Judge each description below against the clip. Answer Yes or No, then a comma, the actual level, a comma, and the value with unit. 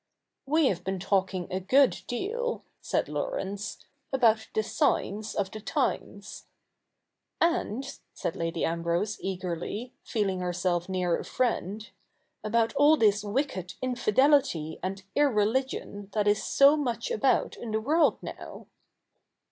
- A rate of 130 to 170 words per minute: Yes, average, 140 wpm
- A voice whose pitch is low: No, high, 215 Hz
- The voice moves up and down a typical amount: No, wide, 5.9 semitones